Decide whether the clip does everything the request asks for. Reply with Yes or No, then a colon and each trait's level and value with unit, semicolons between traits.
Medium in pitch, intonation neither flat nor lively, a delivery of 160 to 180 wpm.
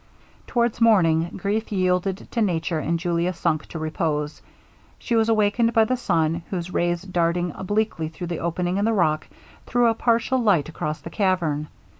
Yes: medium, 180 Hz; average, 4.7 semitones; average, 170 wpm